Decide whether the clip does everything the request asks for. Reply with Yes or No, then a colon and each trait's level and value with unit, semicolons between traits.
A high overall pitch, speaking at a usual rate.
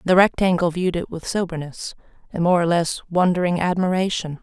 No: medium, 175 Hz; average, 165 wpm